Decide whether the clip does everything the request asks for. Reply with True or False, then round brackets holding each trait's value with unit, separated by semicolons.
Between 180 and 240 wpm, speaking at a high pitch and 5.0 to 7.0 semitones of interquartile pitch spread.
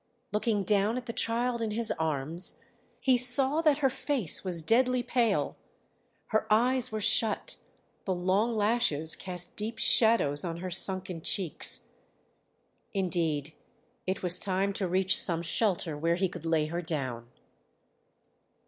False (140 wpm; 195 Hz; 5.4 semitones)